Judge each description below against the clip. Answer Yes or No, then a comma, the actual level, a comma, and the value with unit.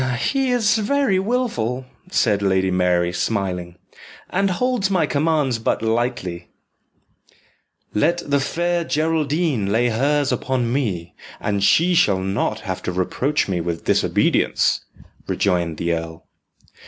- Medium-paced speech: No, slow, 125 wpm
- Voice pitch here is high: No, low, 120 Hz